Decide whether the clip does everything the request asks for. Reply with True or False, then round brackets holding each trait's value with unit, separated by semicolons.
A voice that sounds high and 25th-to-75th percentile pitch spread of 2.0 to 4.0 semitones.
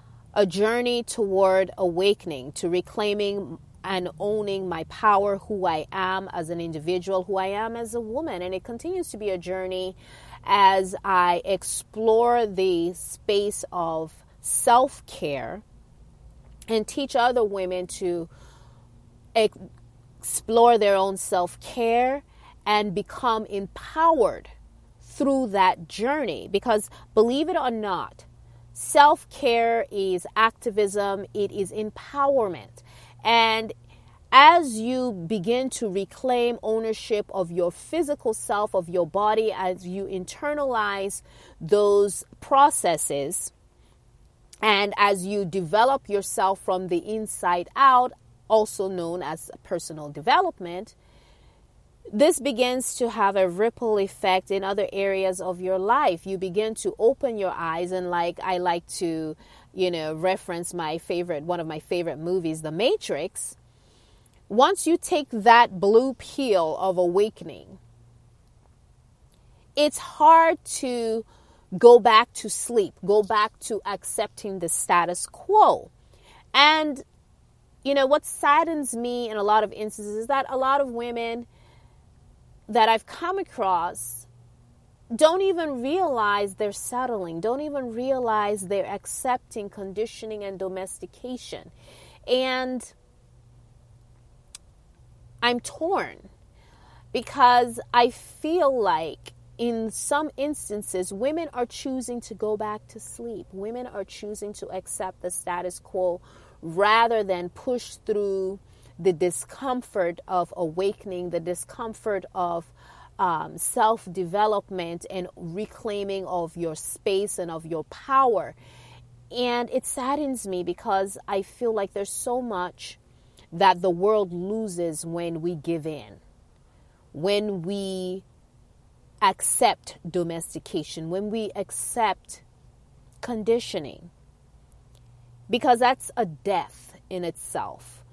False (200 Hz; 5.0 semitones)